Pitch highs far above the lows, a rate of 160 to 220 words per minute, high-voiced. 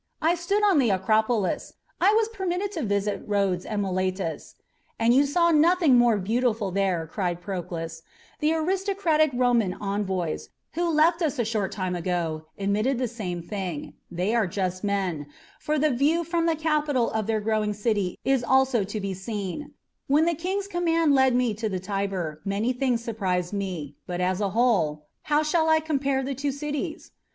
Yes: wide, 7.9 semitones; average, 180 wpm; high, 225 Hz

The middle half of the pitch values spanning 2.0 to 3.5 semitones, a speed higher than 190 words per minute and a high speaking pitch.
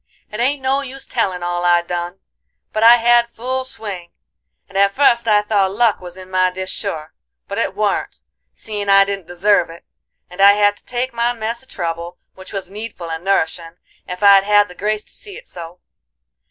No: average, 4.3 semitones; average, 200 wpm; high, 200 Hz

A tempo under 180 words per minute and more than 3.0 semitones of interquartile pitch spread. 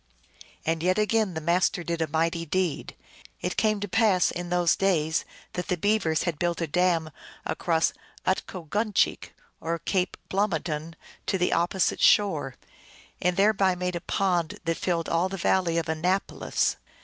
No: average, 160 wpm; narrow, 2.4 semitones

